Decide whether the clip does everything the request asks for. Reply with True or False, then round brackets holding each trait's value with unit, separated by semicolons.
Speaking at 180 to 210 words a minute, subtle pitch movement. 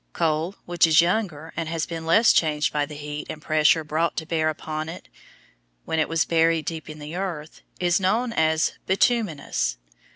True (185 wpm; 1.8 semitones)